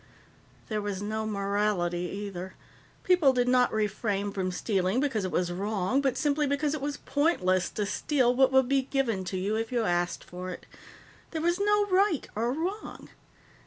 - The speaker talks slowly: No, average, 175 wpm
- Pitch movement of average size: No, wide, 6.4 semitones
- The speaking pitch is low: No, high, 225 Hz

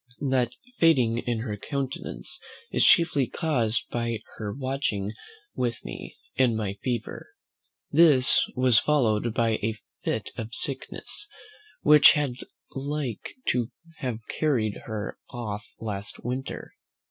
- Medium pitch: No, low, 120 Hz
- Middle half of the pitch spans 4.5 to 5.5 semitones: No, average, 3.7 semitones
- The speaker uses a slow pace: Yes, slow, 120 wpm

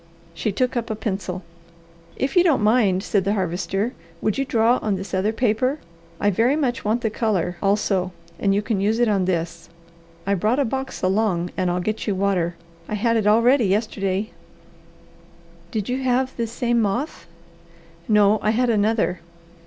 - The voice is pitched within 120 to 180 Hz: No, high, 215 Hz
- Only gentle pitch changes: No, average, 3.5 semitones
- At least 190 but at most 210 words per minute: No, average, 180 wpm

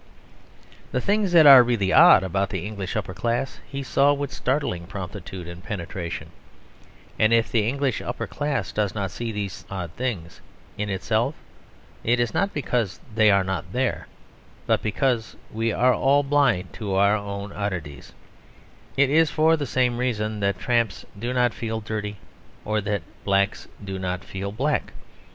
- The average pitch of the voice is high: No, low, 110 Hz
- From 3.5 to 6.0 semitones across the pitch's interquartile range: Yes, average, 4.5 semitones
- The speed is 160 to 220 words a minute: Yes, average, 165 wpm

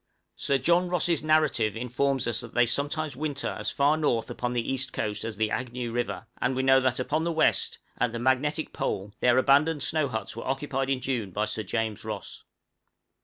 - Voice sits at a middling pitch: No, low, 130 Hz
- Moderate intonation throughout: Yes, average, 3.6 semitones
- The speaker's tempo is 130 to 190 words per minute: No, average, 200 wpm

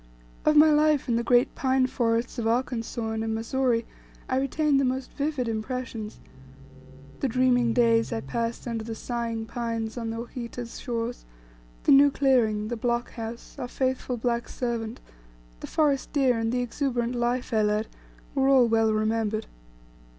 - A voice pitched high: Yes, high, 240 Hz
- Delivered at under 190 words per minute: Yes, average, 165 wpm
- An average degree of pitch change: No, narrow, 2.2 semitones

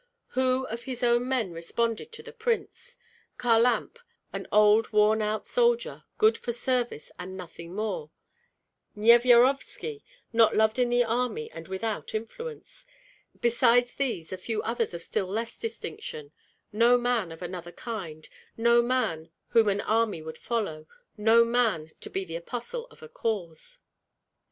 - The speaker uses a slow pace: No, average, 145 wpm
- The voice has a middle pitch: No, high, 230 Hz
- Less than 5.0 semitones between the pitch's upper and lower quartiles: Yes, average, 4.3 semitones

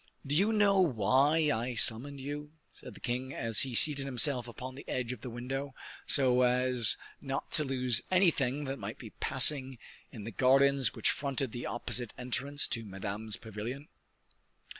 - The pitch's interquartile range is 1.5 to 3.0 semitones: Yes, average, 2.7 semitones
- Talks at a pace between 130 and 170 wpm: Yes, average, 165 wpm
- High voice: No, low, 130 Hz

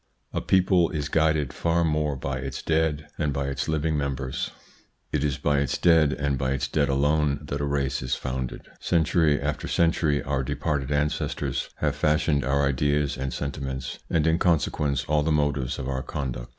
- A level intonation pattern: Yes, narrow, 2.2 semitones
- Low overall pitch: Yes, very low, 75 Hz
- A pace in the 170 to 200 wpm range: Yes, average, 180 wpm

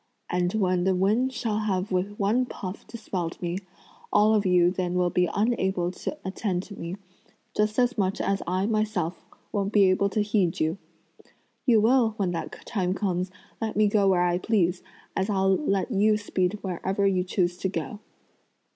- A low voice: No, high, 195 Hz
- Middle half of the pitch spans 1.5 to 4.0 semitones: Yes, average, 2.8 semitones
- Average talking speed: Yes, average, 180 wpm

